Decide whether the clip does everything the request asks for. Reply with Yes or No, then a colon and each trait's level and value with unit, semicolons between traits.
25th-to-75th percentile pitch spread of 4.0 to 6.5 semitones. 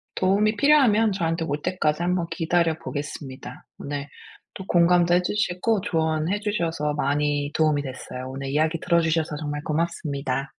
No: average, 3.5 semitones